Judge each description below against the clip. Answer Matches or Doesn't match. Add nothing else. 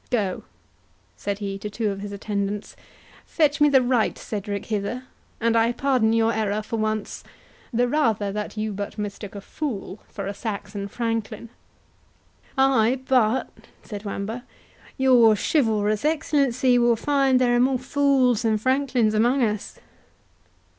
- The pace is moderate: Matches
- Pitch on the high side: Matches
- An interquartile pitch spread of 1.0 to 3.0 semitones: Doesn't match